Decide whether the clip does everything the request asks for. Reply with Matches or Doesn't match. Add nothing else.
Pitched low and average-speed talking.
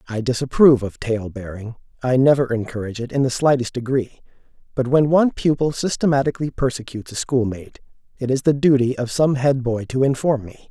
Matches